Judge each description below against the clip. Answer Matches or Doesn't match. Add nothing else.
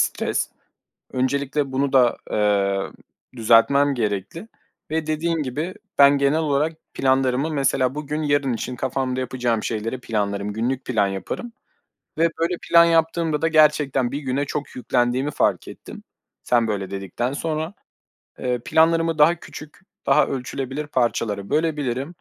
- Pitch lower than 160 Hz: Matches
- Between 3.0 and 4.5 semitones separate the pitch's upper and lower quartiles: Matches